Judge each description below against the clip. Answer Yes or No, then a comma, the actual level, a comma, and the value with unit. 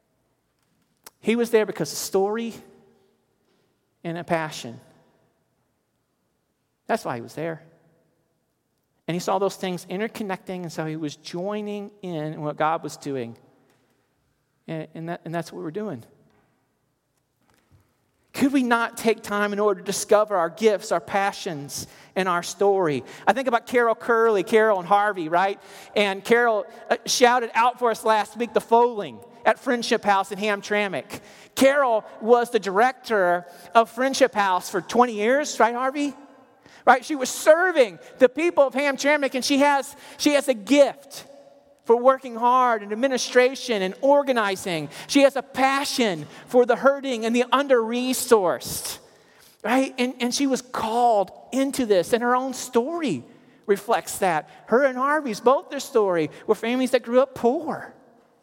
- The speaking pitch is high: Yes, high, 225 Hz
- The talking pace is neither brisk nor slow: Yes, average, 155 wpm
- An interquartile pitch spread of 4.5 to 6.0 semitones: Yes, wide, 5.4 semitones